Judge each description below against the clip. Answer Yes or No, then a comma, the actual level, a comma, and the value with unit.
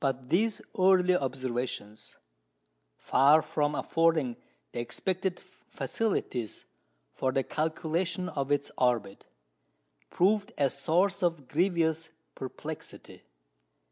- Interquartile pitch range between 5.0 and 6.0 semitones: Yes, wide, 5.5 semitones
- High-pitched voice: No, medium, 155 Hz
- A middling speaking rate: No, slow, 95 wpm